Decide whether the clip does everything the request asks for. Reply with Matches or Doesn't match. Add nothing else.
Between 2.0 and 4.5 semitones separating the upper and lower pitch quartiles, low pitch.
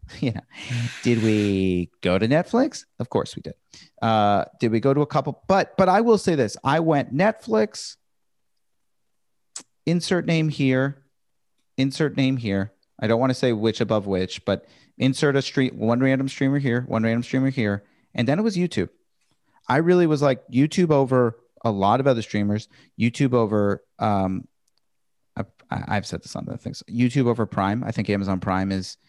Doesn't match